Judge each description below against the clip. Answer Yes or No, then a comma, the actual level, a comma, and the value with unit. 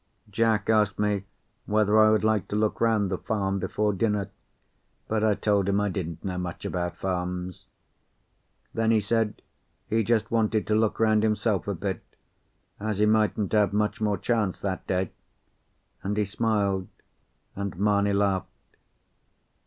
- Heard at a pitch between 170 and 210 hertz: No, low, 105 Hz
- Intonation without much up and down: Yes, narrow, 1.8 semitones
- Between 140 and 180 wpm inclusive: Yes, average, 155 wpm